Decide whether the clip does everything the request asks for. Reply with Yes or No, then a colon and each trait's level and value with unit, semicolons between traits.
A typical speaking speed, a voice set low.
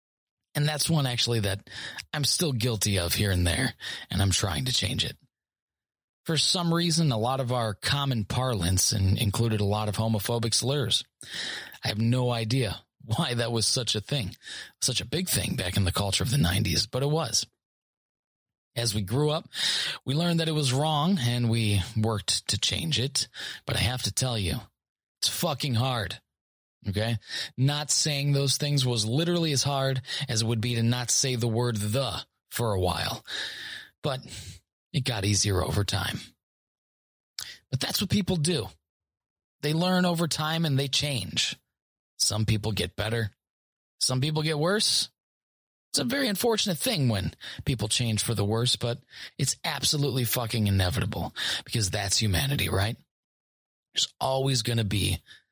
Yes: average, 170 wpm; low, 120 Hz